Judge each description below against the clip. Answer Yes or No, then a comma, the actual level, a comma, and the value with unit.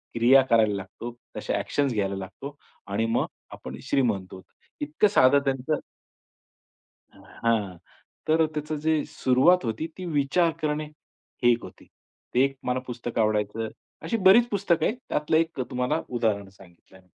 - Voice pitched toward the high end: No, low, 130 Hz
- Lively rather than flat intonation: Yes, wide, 6.0 semitones